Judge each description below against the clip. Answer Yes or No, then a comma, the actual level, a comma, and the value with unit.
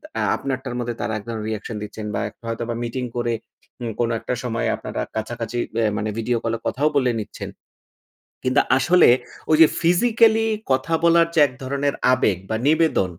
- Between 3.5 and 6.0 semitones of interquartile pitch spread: Yes, average, 4.1 semitones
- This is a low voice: Yes, low, 120 Hz